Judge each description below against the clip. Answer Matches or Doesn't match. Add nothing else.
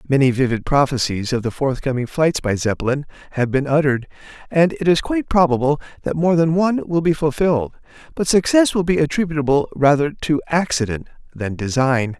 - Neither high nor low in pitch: Matches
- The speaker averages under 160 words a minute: Doesn't match